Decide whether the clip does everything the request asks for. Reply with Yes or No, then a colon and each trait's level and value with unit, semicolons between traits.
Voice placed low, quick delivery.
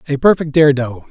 No: medium, 145 Hz; fast, 215 wpm